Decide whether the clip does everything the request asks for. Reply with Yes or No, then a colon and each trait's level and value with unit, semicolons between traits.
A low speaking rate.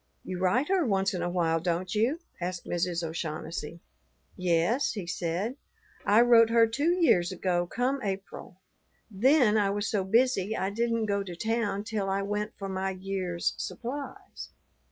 No: average, 160 wpm